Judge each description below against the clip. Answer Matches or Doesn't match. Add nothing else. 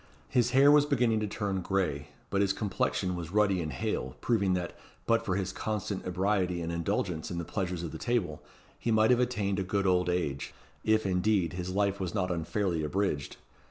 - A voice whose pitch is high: Doesn't match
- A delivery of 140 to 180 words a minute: Doesn't match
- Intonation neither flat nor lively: Matches